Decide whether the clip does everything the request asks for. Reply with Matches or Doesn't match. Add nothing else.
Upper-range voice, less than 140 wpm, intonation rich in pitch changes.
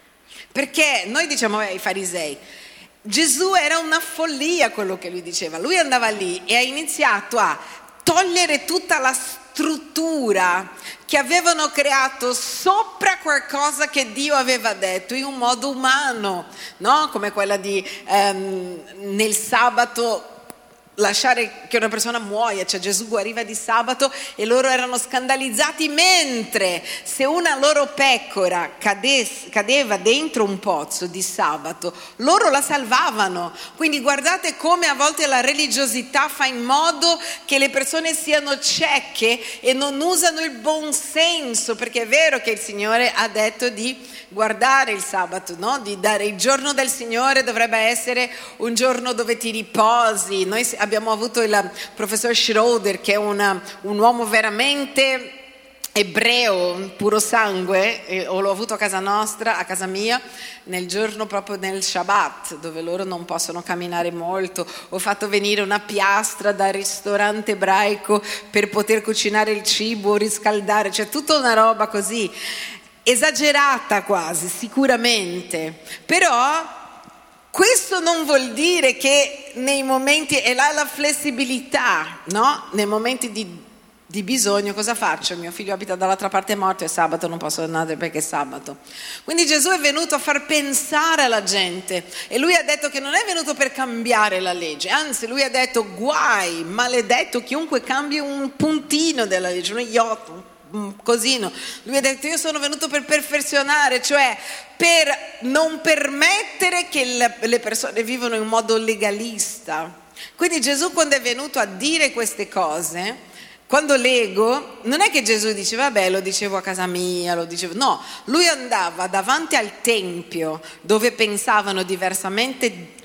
Doesn't match